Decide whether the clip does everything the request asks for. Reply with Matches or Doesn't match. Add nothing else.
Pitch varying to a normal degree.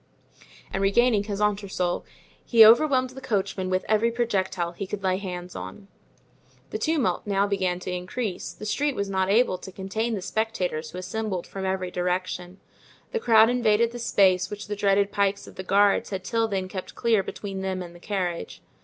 Matches